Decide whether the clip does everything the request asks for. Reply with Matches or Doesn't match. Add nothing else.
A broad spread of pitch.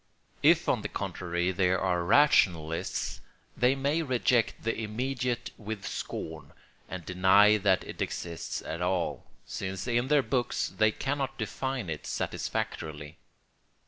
Matches